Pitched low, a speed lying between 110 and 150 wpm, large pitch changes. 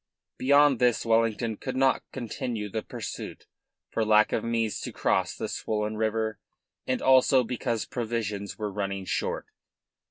No: low, 115 Hz; average, 140 wpm; narrow, 2.6 semitones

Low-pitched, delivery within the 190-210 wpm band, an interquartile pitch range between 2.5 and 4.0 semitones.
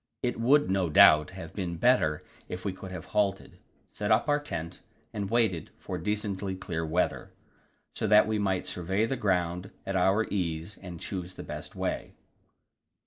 No: very low, 95 Hz; average, 170 wpm; average, 3.1 semitones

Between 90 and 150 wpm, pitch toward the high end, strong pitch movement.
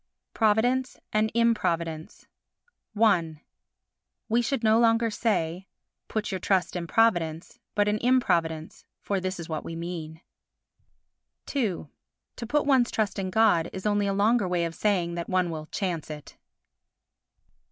No: average, 140 wpm; high, 195 Hz; average, 5.0 semitones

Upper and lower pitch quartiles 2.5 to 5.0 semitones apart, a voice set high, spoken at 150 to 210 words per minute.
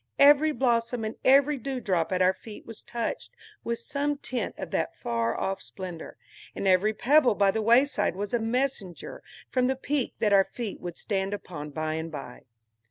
No: wide, 5.6 semitones; high, 220 Hz; average, 180 wpm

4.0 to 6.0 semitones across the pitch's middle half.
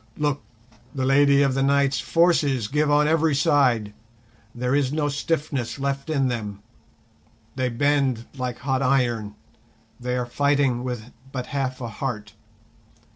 No: narrow, 2.6 semitones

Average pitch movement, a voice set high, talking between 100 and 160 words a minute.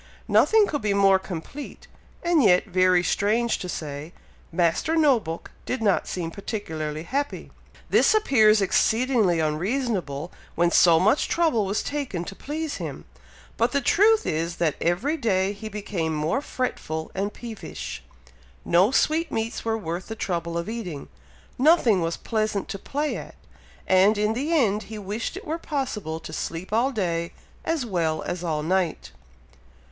No: wide, 6.8 semitones; high, 205 Hz; average, 155 wpm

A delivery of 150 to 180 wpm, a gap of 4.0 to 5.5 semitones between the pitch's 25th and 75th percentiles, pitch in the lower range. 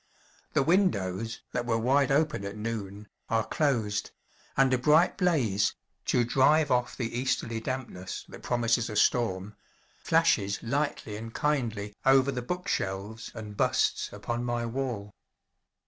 No: average, 140 wpm; average, 4.3 semitones; low, 120 Hz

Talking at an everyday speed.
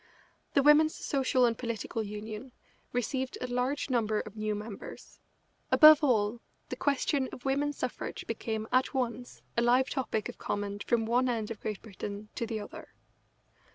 Yes: average, 160 wpm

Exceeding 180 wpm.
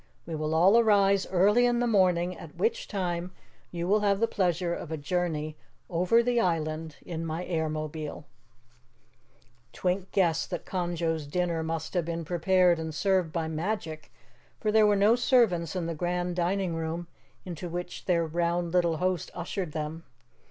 No: average, 165 wpm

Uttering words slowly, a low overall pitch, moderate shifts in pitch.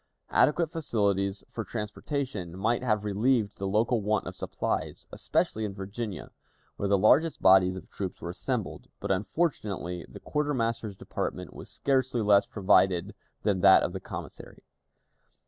No: average, 145 wpm; low, 105 Hz; average, 3.7 semitones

